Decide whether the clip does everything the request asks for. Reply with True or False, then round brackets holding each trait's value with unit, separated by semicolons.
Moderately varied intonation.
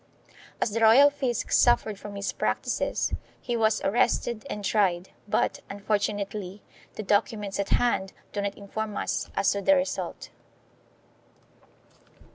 False (2.3 semitones)